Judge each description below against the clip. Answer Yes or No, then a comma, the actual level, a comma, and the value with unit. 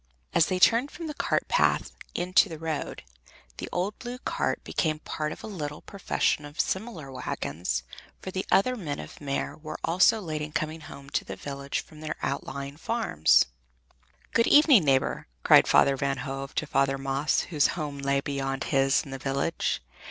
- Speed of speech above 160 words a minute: Yes, average, 180 wpm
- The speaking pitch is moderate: Yes, medium, 150 Hz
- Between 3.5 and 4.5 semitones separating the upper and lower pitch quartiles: No, average, 5.0 semitones